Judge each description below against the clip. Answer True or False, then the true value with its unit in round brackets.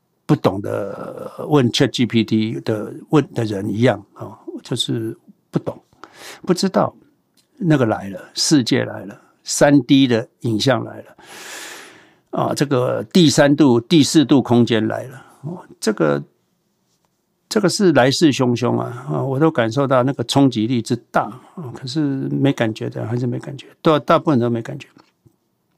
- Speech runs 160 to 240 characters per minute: True (225 characters per minute)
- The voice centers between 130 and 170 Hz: True (135 Hz)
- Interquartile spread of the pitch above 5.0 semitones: True (5.4 semitones)